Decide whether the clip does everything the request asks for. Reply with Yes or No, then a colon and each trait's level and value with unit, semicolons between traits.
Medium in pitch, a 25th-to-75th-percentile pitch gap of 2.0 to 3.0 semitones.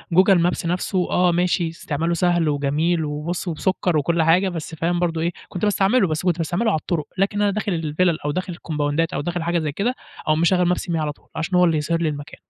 Yes: medium, 170 Hz; narrow, 2.4 semitones